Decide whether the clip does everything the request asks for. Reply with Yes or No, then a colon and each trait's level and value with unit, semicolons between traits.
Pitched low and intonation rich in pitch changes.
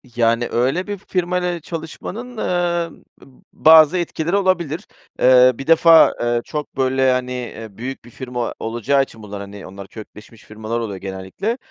Yes: low, 130 Hz; wide, 6.8 semitones